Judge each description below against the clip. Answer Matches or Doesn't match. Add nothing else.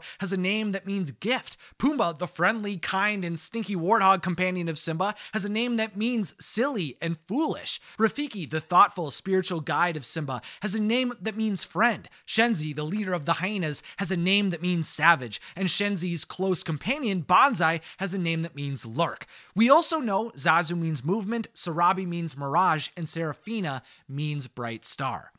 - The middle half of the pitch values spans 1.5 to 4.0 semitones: Doesn't match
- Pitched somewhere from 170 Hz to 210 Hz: Matches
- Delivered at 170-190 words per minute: Matches